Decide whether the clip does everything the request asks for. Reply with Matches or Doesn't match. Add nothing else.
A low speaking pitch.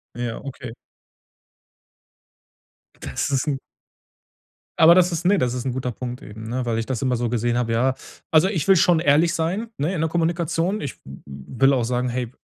Matches